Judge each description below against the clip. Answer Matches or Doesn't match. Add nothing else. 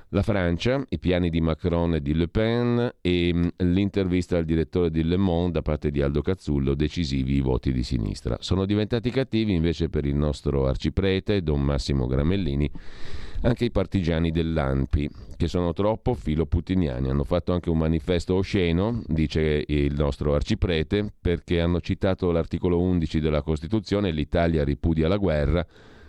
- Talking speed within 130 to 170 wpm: Matches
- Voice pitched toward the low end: Matches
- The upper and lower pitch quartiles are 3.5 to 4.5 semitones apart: Matches